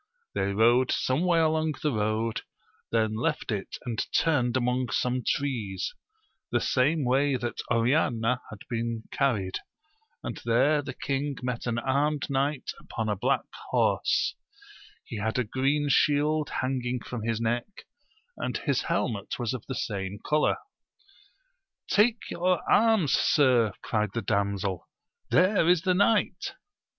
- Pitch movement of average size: Yes, average, 4.6 semitones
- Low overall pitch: Yes, low, 125 Hz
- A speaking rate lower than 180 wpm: Yes, average, 140 wpm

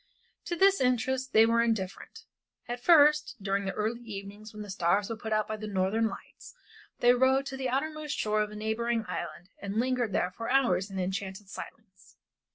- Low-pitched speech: No, high, 220 Hz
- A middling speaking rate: Yes, average, 195 wpm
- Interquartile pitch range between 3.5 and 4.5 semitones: Yes, average, 4.2 semitones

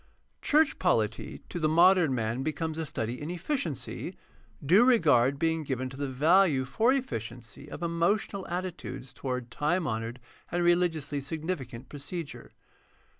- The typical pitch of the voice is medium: Yes, medium, 155 Hz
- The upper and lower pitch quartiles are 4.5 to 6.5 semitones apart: Yes, average, 5.3 semitones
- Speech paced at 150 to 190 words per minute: No, average, 140 wpm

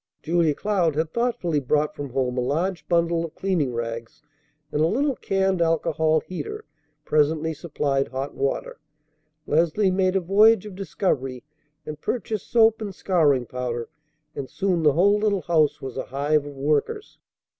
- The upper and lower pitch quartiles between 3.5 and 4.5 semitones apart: No, average, 5.3 semitones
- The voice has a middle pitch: Yes, medium, 160 Hz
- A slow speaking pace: No, average, 155 wpm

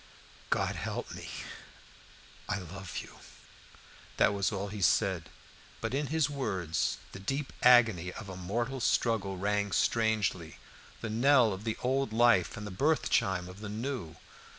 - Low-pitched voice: Yes, low, 105 Hz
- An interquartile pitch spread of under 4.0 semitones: No, average, 4.4 semitones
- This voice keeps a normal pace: Yes, average, 150 wpm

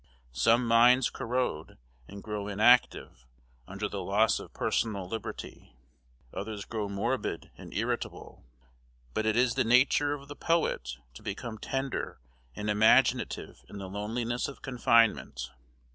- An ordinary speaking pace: No, slow, 130 wpm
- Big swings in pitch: No, average, 3.6 semitones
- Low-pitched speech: Yes, low, 115 Hz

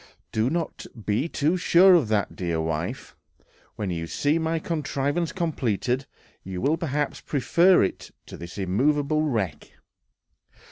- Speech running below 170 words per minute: Yes, slow, 135 wpm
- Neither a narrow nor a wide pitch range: No, wide, 8.2 semitones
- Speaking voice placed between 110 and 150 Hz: Yes, medium, 140 Hz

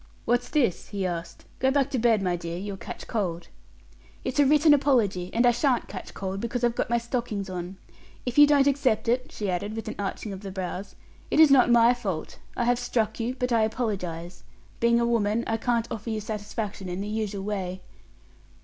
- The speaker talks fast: Yes, fast, 210 wpm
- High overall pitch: Yes, high, 220 Hz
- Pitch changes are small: No, average, 4.0 semitones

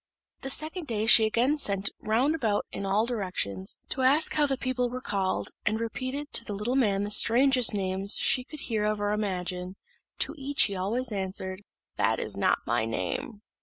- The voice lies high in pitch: Yes, high, 220 Hz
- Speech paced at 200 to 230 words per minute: No, average, 190 wpm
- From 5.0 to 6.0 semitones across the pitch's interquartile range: No, average, 4.6 semitones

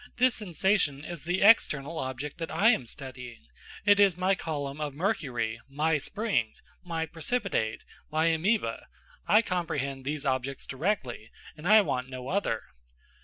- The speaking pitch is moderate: Yes, medium, 155 Hz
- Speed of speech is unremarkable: Yes, average, 145 wpm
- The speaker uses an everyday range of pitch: No, wide, 6.4 semitones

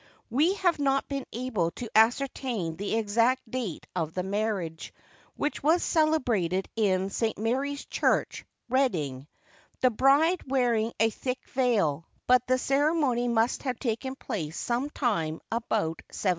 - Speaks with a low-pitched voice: No, high, 235 Hz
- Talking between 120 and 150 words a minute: Yes, average, 140 wpm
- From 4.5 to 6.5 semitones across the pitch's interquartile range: Yes, average, 5.0 semitones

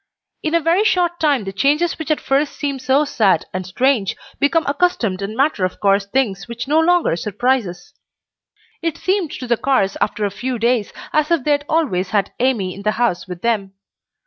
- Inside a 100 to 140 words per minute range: No, average, 200 wpm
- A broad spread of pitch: Yes, wide, 7.2 semitones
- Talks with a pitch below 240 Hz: No, very high, 255 Hz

